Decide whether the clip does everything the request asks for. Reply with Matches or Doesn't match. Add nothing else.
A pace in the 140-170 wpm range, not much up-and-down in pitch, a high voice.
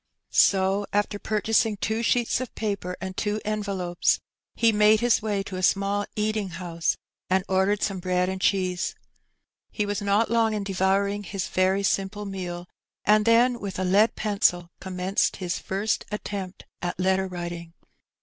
Matches